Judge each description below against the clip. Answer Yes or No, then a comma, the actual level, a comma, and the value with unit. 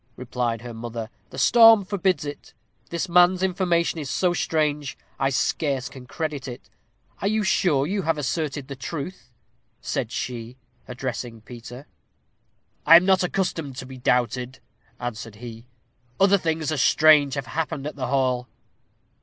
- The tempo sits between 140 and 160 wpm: Yes, average, 150 wpm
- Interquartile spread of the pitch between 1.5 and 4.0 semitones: No, average, 5.3 semitones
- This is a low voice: No, medium, 145 Hz